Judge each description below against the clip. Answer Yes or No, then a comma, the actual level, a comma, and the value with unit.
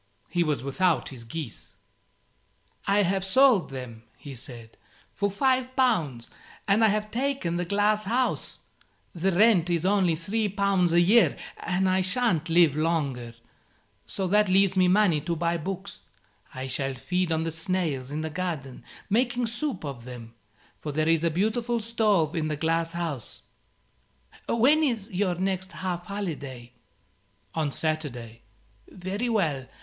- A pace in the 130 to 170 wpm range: Yes, average, 150 wpm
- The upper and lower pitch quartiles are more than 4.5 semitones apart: Yes, average, 5.1 semitones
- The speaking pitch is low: No, medium, 175 Hz